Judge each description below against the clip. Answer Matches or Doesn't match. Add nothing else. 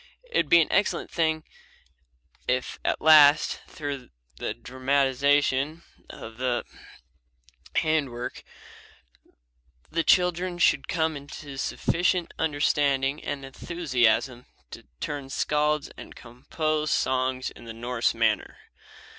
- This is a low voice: Doesn't match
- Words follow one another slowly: Matches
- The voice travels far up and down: Doesn't match